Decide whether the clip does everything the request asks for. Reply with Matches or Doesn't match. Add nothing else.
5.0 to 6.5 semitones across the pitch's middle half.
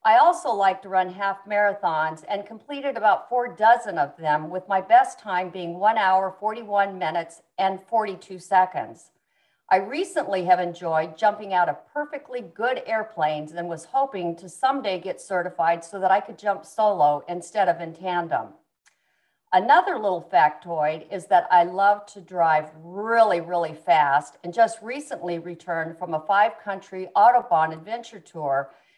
Doesn't match